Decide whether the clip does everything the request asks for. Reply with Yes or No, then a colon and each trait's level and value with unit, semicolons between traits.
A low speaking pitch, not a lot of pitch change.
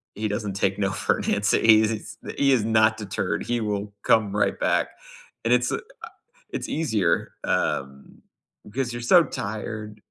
Yes: low, 110 Hz; narrow, 1.7 semitones